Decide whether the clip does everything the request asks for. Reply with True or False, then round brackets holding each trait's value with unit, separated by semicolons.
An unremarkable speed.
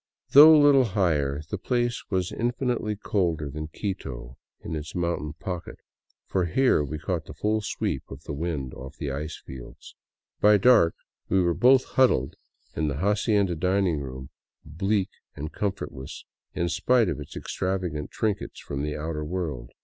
True (160 wpm)